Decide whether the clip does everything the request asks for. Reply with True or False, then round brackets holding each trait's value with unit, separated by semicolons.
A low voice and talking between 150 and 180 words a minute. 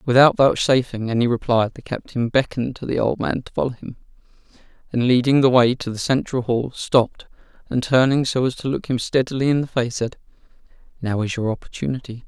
False (125 Hz; 190 wpm)